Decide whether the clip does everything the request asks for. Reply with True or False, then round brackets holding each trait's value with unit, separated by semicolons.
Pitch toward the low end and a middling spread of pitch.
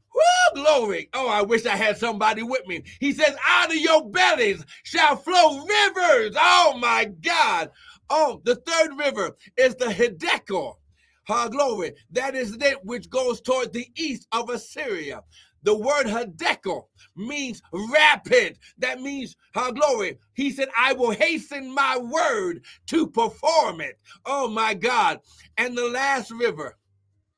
False (260 Hz; 4.9 semitones)